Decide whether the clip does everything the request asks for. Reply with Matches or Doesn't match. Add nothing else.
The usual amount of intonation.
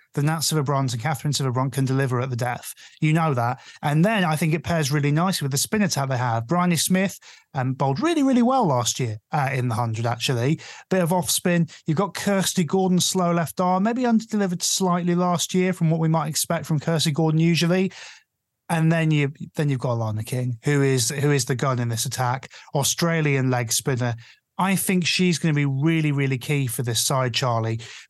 Matches